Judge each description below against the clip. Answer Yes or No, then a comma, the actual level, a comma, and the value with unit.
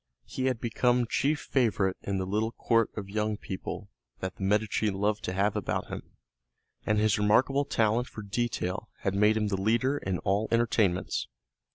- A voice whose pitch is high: No, low, 105 Hz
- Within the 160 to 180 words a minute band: Yes, average, 175 wpm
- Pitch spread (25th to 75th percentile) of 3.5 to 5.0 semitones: No, average, 2.8 semitones